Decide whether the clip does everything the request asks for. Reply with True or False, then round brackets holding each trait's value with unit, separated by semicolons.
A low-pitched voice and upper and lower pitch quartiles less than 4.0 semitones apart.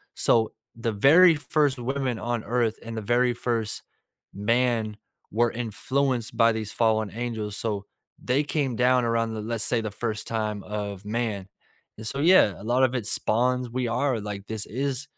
True (115 Hz; 2.7 semitones)